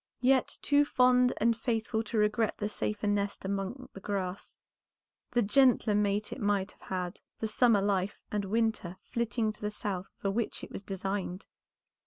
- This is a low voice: No, high, 210 Hz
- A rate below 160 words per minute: No, average, 170 wpm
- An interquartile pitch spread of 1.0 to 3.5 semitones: Yes, average, 2.8 semitones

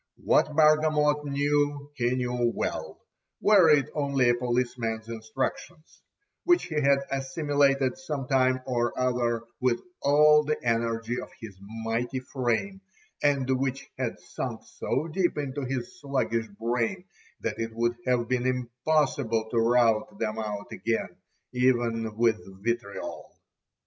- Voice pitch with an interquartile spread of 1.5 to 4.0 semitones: Yes, average, 3.7 semitones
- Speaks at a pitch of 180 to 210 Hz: No, low, 125 Hz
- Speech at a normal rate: No, slow, 130 wpm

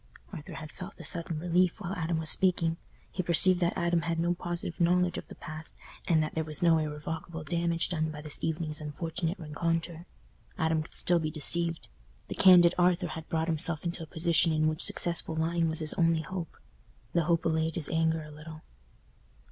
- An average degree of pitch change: No, narrow, 1.6 semitones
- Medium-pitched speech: Yes, medium, 165 Hz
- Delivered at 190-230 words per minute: Yes, average, 195 wpm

